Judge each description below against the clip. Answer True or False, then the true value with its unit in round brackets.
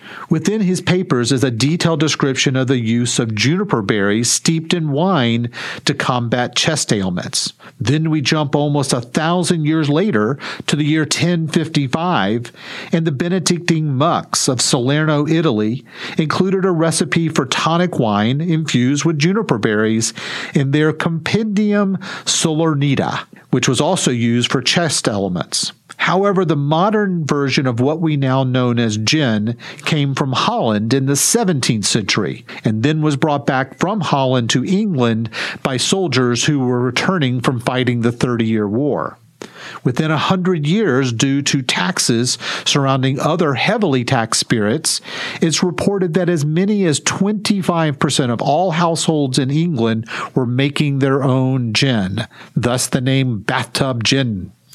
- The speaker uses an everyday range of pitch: True (4.9 semitones)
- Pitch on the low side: False (145 Hz)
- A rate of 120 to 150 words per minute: True (145 wpm)